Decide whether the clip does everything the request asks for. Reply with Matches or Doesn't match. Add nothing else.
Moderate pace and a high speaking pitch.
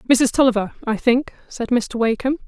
Matches